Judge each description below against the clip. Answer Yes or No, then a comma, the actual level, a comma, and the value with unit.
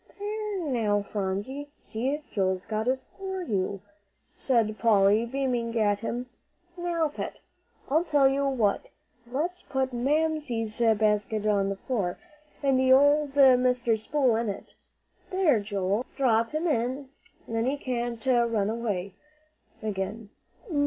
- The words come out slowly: Yes, slow, 125 wpm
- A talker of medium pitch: No, high, 240 Hz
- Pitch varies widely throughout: No, average, 4.7 semitones